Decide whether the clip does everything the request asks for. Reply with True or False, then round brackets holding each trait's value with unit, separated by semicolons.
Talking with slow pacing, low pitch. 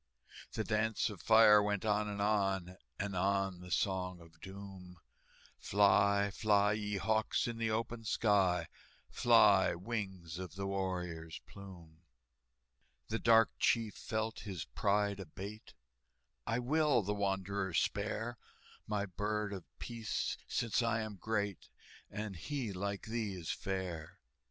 True (130 wpm; 100 Hz)